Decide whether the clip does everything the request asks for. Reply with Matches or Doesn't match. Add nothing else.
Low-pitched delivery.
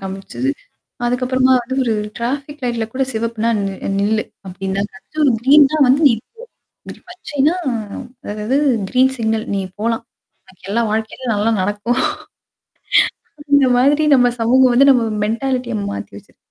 Doesn't match